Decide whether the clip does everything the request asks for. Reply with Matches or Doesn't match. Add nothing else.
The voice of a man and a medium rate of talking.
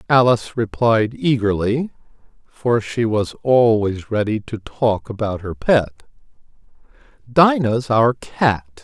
Doesn't match